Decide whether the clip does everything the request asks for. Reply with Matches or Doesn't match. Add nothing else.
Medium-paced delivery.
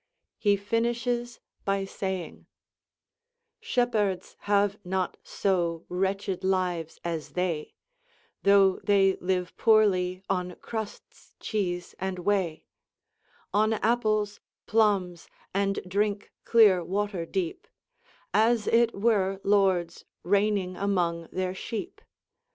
Doesn't match